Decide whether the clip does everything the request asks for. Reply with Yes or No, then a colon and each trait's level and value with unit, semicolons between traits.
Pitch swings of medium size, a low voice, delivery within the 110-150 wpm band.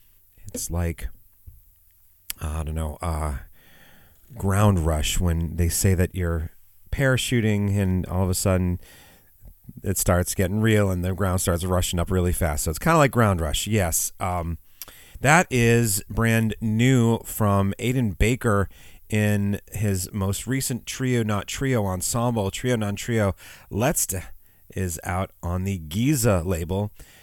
Yes: average, 3.7 semitones; very low, 95 Hz; average, 145 wpm